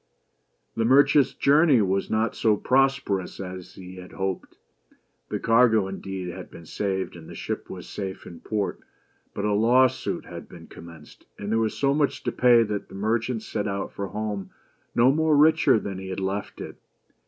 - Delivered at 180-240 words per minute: Yes, average, 185 wpm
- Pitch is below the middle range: Yes, low, 105 Hz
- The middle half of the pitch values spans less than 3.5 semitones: No, average, 4.7 semitones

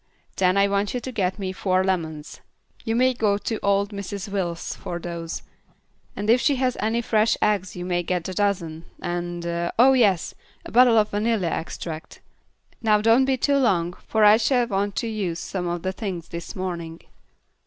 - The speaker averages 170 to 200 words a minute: Yes, average, 185 wpm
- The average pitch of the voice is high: Yes, high, 200 Hz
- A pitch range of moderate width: Yes, average, 4.2 semitones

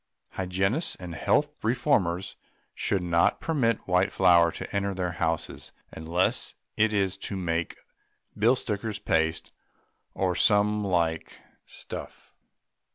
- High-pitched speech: No, very low, 95 Hz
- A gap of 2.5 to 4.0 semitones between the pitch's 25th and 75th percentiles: Yes, average, 3.6 semitones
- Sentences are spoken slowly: Yes, slow, 115 wpm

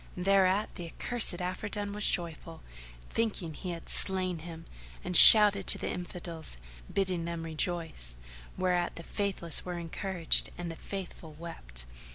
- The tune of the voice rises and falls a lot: No, narrow, 2.6 semitones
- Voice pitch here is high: No, medium, 175 Hz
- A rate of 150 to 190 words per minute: No, average, 140 wpm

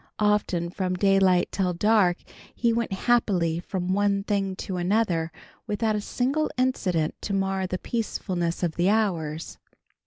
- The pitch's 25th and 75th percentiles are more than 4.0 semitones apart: No, average, 3.1 semitones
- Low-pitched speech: No, high, 195 Hz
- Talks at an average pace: Yes, average, 145 wpm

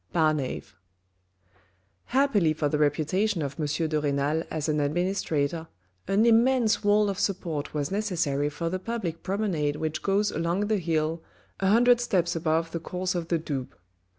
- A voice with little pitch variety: No, average, 4.7 semitones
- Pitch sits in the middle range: Yes, medium, 170 Hz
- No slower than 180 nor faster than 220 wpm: No, average, 160 wpm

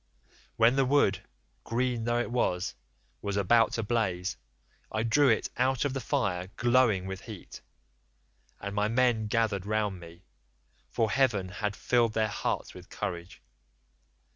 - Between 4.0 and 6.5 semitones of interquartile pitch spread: No, average, 3.6 semitones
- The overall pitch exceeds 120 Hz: No, low, 110 Hz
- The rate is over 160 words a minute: No, average, 145 wpm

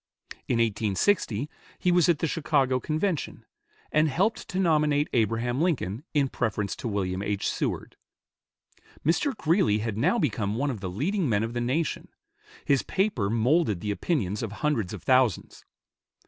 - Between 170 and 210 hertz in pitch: No, low, 130 Hz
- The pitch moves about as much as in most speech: No, wide, 6.9 semitones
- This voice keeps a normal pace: Yes, average, 155 wpm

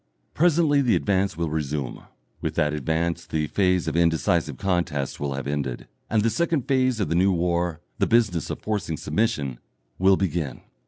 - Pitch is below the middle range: Yes, very low, 85 Hz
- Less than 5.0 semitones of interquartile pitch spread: No, wide, 5.6 semitones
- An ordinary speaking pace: Yes, average, 170 wpm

